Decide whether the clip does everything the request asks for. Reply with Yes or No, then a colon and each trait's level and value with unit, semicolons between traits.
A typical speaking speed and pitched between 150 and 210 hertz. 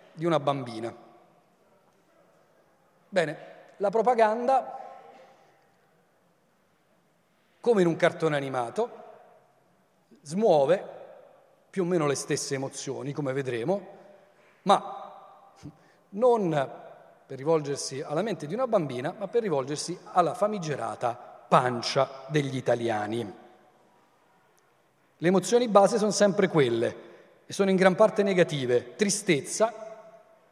No: slow, 100 wpm; medium, 185 Hz